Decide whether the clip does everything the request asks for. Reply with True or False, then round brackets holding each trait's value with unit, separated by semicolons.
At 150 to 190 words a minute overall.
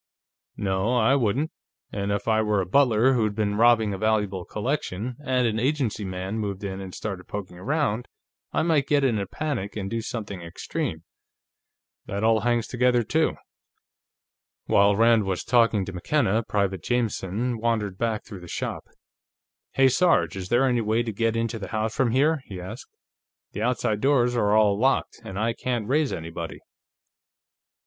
True (165 wpm)